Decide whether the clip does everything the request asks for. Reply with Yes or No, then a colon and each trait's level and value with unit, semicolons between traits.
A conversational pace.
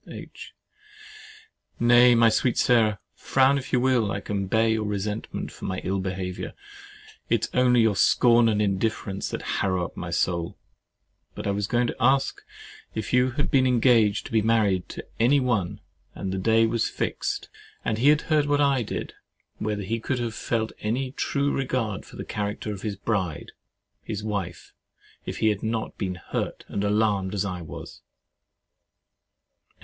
Yes: average, 170 wpm